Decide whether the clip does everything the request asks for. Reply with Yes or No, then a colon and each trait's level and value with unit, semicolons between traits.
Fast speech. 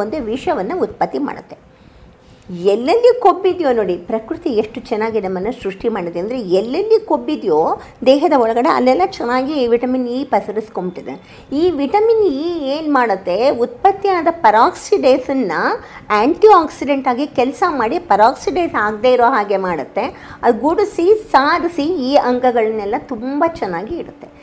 Yes: fast, 115 wpm